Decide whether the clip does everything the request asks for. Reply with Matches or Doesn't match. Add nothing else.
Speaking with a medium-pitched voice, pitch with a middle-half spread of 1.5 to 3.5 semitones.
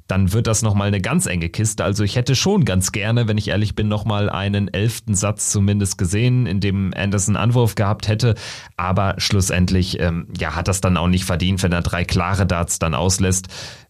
Doesn't match